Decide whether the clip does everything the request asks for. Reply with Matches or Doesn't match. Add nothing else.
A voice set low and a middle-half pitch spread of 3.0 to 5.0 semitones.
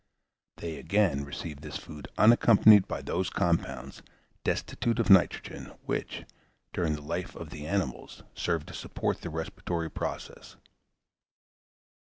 Matches